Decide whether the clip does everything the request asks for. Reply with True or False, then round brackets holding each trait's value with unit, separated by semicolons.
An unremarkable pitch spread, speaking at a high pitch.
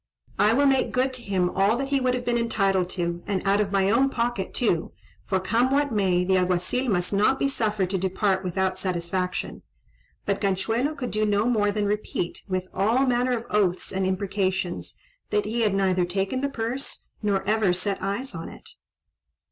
True (4.1 semitones; 200 Hz)